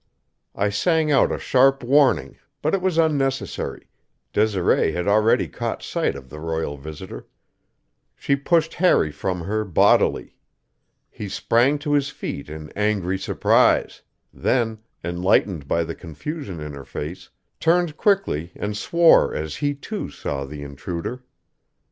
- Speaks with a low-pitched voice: Yes, low, 105 Hz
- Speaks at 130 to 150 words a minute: Yes, average, 140 wpm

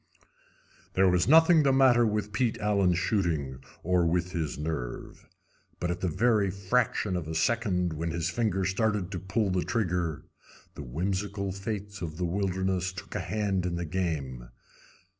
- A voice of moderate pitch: No, very low, 95 Hz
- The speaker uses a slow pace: No, average, 160 wpm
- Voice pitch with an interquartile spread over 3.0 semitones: Yes, average, 3.4 semitones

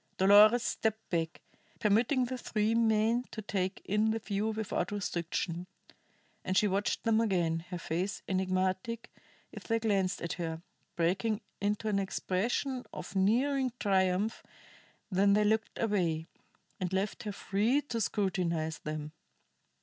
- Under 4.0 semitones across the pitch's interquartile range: Yes, average, 3.2 semitones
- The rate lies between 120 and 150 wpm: Yes, slow, 135 wpm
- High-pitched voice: Yes, high, 200 Hz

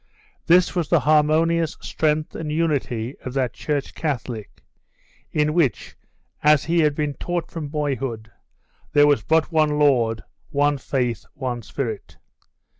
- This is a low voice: No, medium, 150 Hz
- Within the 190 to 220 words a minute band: No, slow, 135 wpm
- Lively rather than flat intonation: No, average, 3.2 semitones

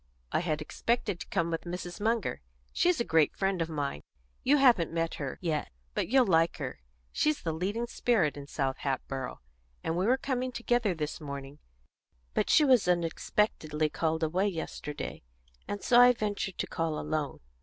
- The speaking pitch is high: No, medium, 170 Hz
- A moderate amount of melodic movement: No, wide, 6.9 semitones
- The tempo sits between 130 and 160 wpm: No, average, 175 wpm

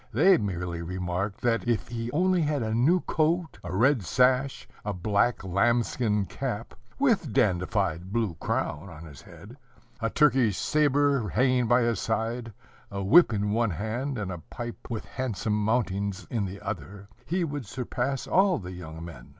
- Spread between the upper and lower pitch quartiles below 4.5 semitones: No, average, 5.2 semitones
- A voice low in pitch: Yes, low, 110 Hz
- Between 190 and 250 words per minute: No, average, 165 wpm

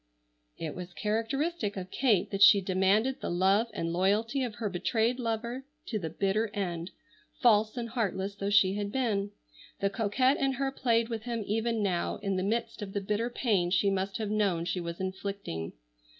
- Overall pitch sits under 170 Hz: No, high, 205 Hz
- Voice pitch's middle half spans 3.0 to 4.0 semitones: Yes, average, 3.3 semitones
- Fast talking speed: No, average, 185 wpm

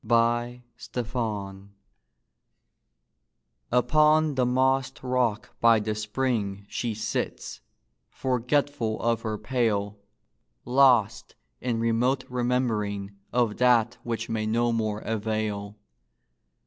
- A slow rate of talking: Yes, slow, 95 wpm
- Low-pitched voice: Yes, low, 115 Hz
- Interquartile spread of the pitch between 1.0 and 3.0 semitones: Yes, narrow, 2.6 semitones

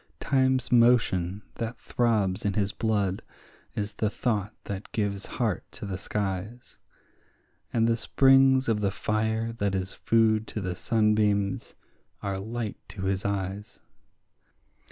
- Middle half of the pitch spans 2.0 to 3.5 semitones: Yes, average, 2.7 semitones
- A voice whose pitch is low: Yes, low, 105 Hz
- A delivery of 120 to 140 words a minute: Yes, slow, 135 wpm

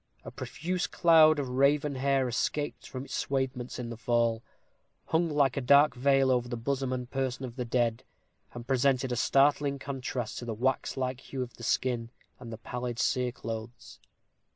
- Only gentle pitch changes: Yes, narrow, 2.3 semitones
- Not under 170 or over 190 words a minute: Yes, average, 175 wpm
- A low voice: Yes, low, 130 Hz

